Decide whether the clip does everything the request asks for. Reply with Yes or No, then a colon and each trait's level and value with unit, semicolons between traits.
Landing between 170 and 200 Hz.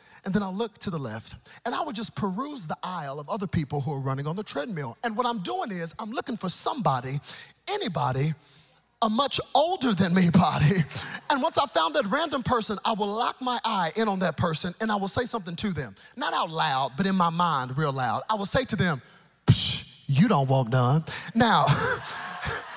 Yes: high, 190 Hz